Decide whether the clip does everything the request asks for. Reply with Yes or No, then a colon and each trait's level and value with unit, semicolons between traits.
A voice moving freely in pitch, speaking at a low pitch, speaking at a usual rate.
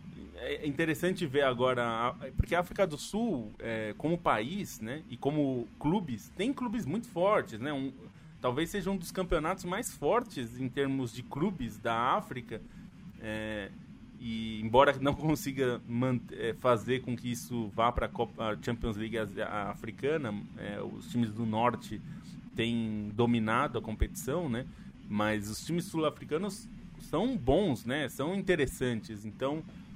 Yes: wide, 6.9 semitones; low, 130 Hz; average, 145 wpm